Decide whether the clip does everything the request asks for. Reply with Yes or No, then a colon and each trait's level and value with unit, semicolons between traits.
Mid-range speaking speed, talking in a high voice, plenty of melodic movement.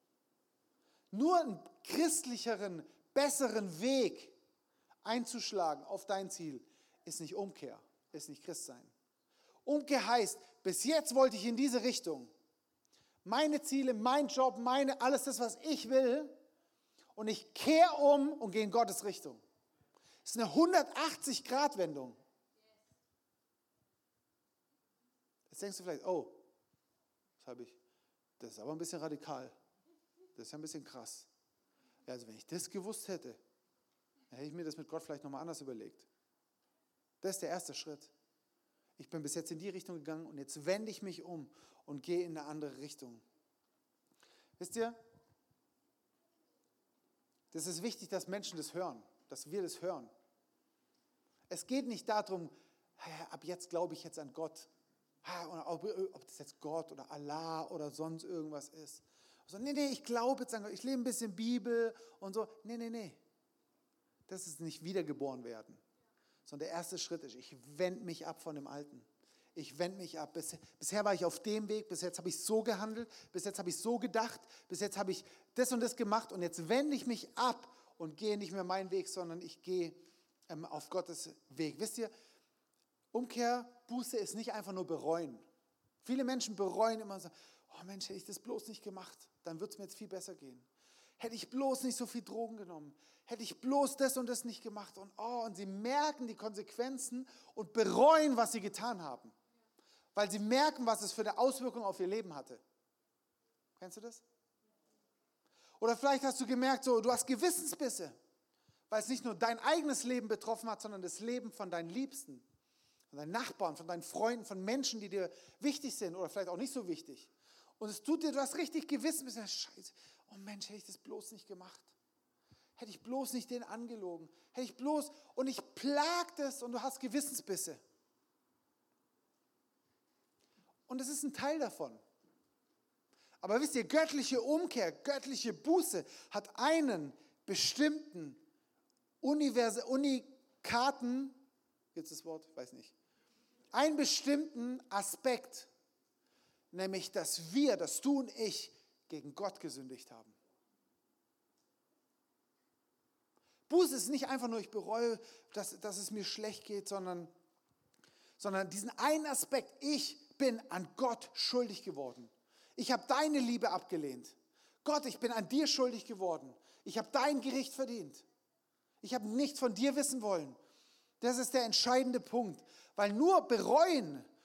Yes: average, 160 wpm; high, 225 Hz; wide, 6.8 semitones